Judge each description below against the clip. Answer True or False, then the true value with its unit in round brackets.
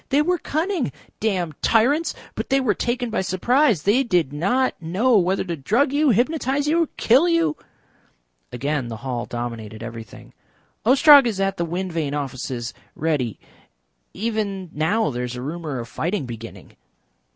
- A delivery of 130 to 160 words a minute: True (155 wpm)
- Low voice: False (190 Hz)